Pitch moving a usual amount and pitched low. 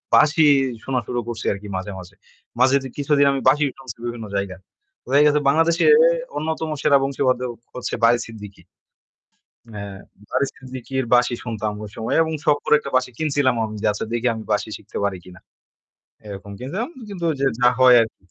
Yes: average, 4.6 semitones; low, 125 Hz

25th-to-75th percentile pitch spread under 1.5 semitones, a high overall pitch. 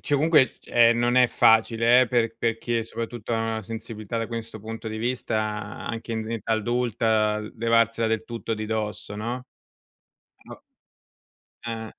No: narrow, 1.1 semitones; low, 115 Hz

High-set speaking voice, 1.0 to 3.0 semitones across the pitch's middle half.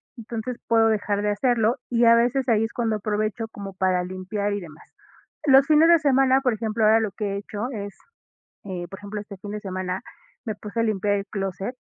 Yes: high, 215 Hz; average, 2.7 semitones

